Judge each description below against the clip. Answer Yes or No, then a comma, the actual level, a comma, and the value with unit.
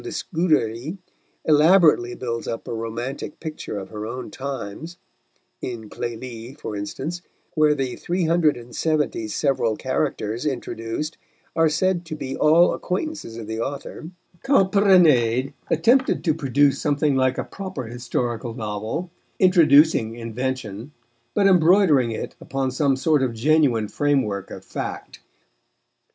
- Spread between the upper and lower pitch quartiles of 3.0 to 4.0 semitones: No, wide, 5.6 semitones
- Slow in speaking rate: Yes, slow, 130 wpm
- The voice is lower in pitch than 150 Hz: Yes, low, 135 Hz